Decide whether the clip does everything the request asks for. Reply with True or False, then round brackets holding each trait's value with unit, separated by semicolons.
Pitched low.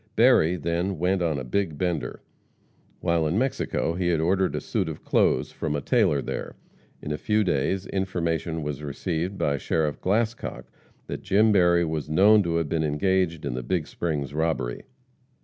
True (85 Hz)